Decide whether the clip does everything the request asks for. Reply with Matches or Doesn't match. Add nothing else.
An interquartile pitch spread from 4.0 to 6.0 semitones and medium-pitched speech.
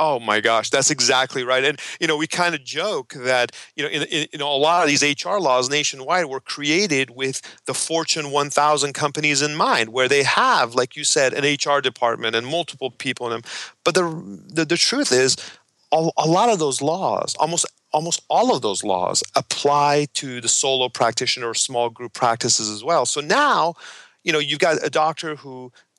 Doesn't match